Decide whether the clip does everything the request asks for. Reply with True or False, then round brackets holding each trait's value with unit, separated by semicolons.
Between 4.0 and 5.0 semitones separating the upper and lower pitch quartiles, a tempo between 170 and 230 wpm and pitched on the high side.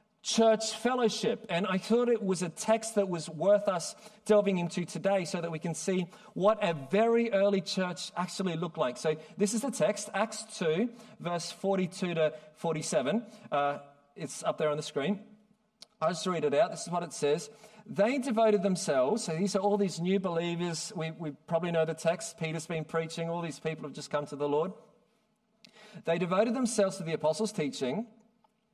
True (4.7 semitones; 190 wpm; 195 Hz)